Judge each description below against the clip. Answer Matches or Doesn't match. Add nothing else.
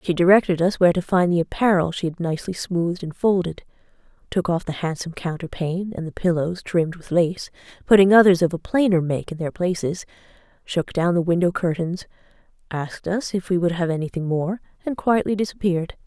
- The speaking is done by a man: Doesn't match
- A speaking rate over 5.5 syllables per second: Matches